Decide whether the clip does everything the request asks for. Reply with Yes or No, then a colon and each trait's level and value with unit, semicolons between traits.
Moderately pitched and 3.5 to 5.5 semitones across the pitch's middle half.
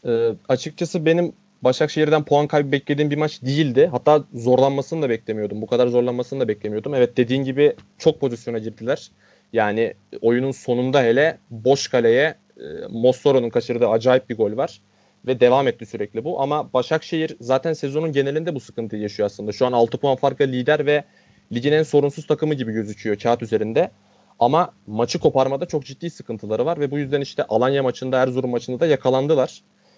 No: low, 130 Hz; average, 4.0 semitones